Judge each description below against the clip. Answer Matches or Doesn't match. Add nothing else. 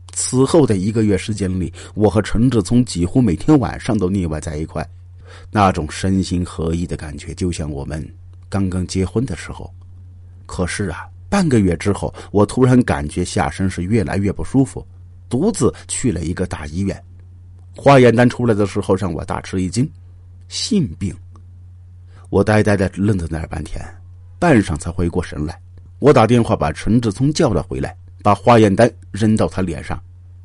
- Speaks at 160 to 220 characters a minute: Doesn't match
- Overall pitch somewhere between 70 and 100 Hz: Matches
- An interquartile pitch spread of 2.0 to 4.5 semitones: Matches